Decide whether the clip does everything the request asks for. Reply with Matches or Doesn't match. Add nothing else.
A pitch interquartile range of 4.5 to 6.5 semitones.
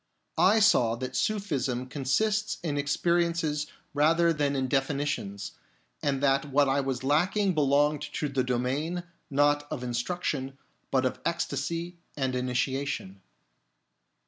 Doesn't match